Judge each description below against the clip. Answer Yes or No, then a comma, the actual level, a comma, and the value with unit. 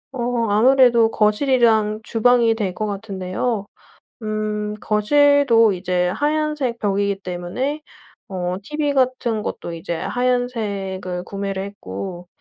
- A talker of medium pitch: No, high, 215 Hz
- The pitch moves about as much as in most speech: Yes, average, 4.2 semitones